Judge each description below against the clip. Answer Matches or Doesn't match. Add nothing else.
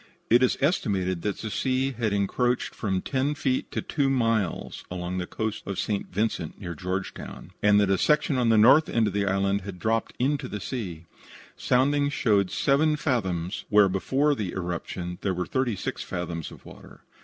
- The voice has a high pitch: Doesn't match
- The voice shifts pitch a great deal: Matches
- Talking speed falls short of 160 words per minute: Doesn't match